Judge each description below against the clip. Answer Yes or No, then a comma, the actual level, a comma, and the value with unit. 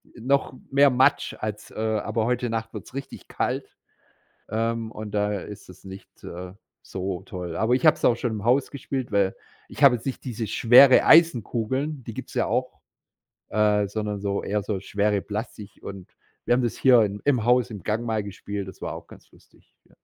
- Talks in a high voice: No, low, 110 Hz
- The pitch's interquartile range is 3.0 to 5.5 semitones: Yes, average, 3.4 semitones